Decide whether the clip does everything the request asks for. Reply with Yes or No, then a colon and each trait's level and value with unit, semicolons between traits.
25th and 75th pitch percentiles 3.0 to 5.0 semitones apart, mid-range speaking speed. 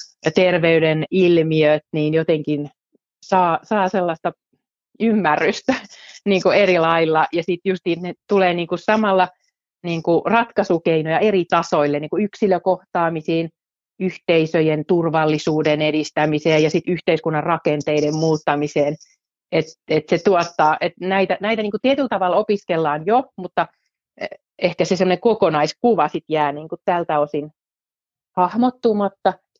Yes: average, 3.4 semitones; average, 125 wpm